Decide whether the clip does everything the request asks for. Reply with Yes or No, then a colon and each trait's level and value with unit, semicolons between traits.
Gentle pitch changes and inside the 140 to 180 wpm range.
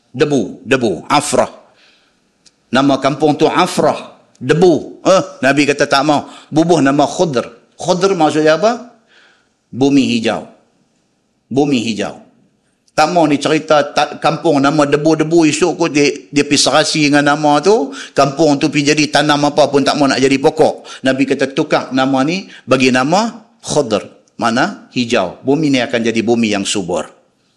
Yes: narrow, 2.3 semitones; average, 150 wpm